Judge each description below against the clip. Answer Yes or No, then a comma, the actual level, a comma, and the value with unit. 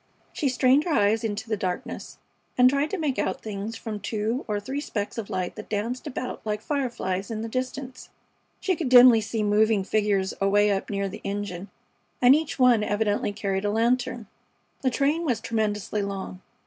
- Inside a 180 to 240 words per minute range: Yes, average, 185 wpm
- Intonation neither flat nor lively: Yes, average, 3.7 semitones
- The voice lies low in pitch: No, high, 220 Hz